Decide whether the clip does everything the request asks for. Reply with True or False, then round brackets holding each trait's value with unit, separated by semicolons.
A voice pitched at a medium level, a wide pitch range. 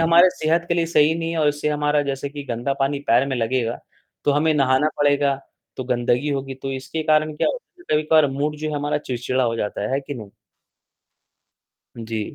False (145 Hz; 2.9 semitones)